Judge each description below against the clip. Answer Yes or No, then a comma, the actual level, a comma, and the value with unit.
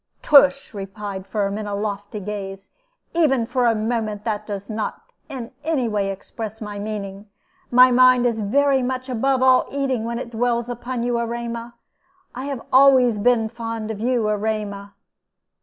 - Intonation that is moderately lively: Yes, average, 3.2 semitones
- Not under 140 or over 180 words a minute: Yes, average, 160 wpm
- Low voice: No, high, 230 Hz